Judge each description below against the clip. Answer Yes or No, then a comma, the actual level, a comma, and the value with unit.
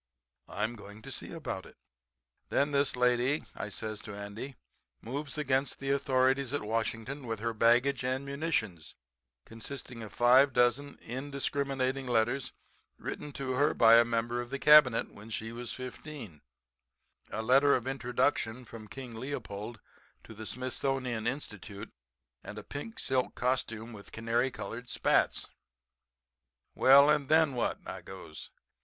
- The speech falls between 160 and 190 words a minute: No, average, 145 wpm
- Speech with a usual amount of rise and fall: Yes, average, 3.4 semitones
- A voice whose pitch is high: No, low, 125 Hz